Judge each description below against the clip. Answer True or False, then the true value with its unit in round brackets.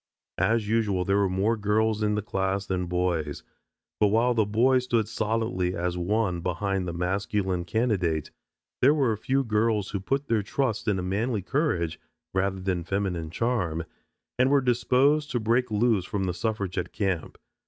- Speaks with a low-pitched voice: True (105 Hz)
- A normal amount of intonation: True (3.9 semitones)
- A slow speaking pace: False (165 wpm)